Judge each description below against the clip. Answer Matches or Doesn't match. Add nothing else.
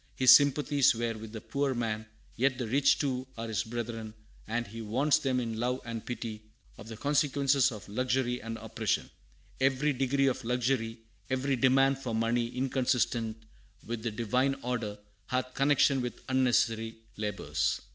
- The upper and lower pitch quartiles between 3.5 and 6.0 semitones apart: Doesn't match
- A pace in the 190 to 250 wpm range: Doesn't match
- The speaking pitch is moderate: Doesn't match